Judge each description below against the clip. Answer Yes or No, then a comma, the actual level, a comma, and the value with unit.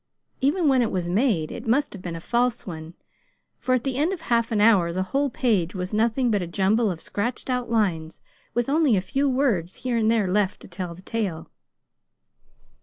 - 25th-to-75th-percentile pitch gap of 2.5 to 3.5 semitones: No, wide, 5.5 semitones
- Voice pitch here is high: Yes, high, 220 Hz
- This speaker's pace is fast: Yes, fast, 210 wpm